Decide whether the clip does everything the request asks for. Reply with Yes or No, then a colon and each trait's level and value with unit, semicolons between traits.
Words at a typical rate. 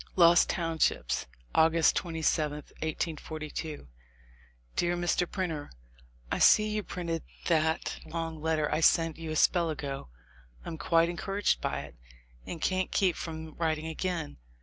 No: slow, 130 wpm